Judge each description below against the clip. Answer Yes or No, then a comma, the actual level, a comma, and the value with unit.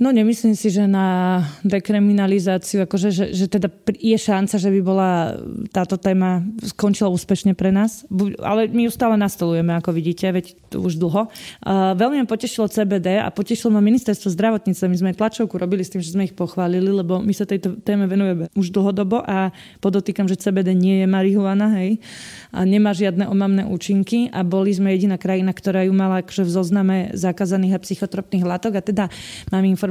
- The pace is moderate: No, fast, 180 wpm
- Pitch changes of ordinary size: No, narrow, 1.7 semitones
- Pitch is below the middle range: No, high, 195 Hz